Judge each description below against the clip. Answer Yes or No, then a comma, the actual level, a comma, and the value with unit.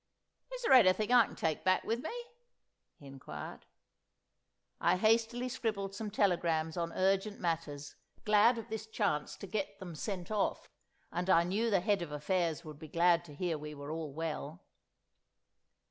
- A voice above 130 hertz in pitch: Yes, medium, 185 Hz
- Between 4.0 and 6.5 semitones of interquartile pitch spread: Yes, average, 4.9 semitones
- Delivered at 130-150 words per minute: No, average, 165 wpm